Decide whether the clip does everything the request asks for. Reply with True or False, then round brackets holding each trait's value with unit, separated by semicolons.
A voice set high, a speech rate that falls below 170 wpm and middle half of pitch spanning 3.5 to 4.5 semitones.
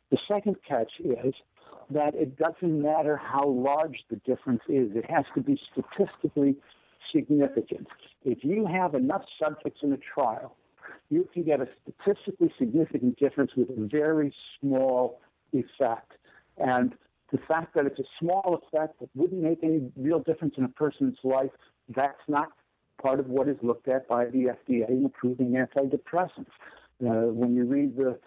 False (140 Hz; 160 wpm; 3.9 semitones)